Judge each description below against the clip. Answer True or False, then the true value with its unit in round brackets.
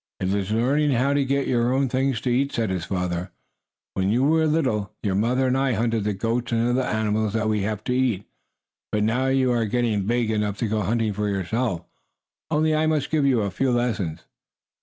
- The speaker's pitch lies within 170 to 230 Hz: False (115 Hz)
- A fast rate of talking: True (215 wpm)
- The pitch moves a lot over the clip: False (3.9 semitones)